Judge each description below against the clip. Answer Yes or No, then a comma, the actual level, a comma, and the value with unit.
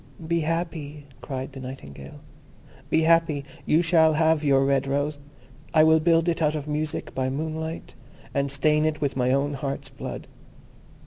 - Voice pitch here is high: No, medium, 150 Hz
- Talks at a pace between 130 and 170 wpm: Yes, average, 165 wpm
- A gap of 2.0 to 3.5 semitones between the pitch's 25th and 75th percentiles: Yes, narrow, 2.5 semitones